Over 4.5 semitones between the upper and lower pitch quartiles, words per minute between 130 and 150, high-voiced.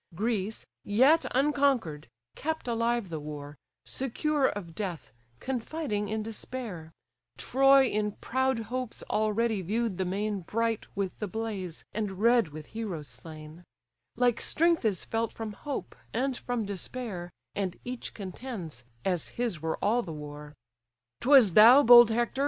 Yes: average, 5.0 semitones; average, 140 wpm; high, 220 Hz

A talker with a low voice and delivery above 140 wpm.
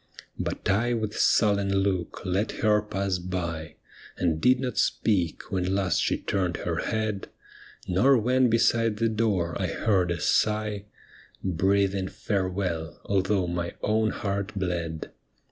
No: low, 100 Hz; slow, 135 wpm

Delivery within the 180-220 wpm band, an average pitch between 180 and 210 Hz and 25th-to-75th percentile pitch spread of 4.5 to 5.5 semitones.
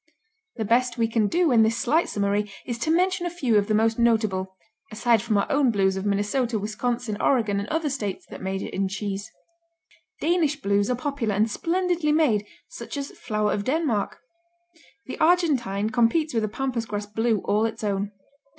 No: average, 185 wpm; high, 225 Hz; average, 5.1 semitones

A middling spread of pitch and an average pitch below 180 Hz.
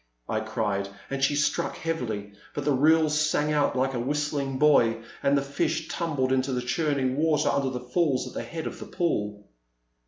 Yes: average, 3.3 semitones; medium, 140 Hz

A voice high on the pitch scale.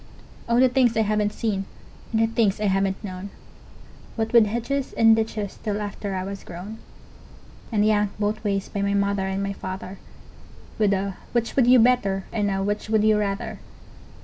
Yes: high, 210 Hz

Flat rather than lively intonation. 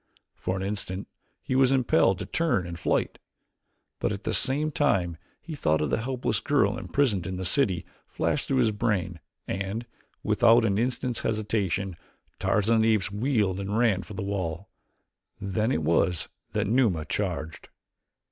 No: average, 4.4 semitones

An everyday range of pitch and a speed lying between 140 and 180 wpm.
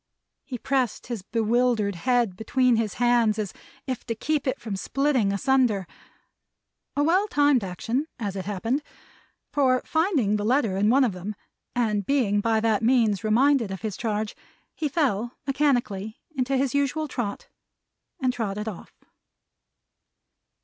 Yes: average, 4.2 semitones; average, 145 wpm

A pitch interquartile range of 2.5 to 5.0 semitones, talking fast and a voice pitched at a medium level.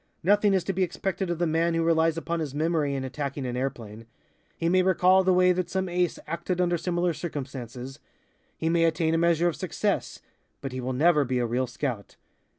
Yes: average, 4.4 semitones; fast, 210 wpm; medium, 165 Hz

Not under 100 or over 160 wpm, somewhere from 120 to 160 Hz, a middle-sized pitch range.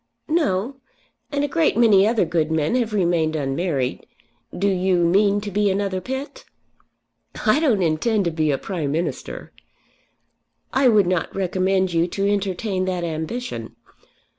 No: average, 145 wpm; high, 190 Hz; average, 4.0 semitones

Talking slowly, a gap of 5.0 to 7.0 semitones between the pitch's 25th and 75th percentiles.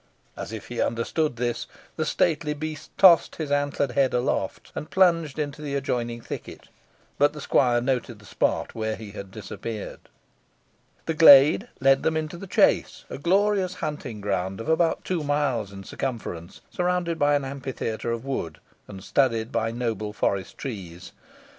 No: average, 160 wpm; wide, 5.4 semitones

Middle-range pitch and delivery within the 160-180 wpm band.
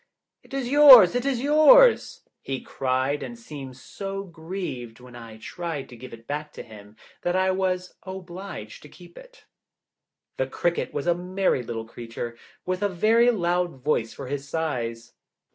Yes: medium, 170 Hz; average, 165 wpm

